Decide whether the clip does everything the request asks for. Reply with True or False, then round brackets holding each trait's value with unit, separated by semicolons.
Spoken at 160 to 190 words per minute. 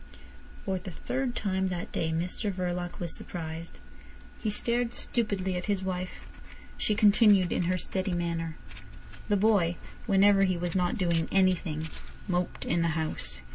False (150 wpm)